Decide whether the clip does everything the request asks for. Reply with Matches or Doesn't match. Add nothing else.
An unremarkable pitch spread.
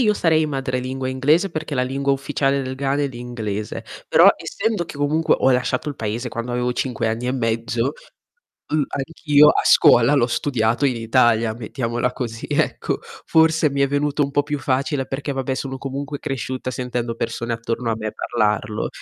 Matches